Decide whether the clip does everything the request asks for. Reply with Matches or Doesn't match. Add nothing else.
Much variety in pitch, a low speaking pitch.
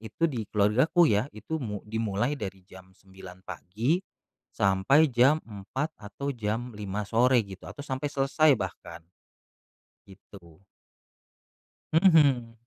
Matches